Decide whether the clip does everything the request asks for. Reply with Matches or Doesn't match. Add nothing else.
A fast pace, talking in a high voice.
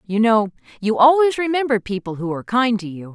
Matches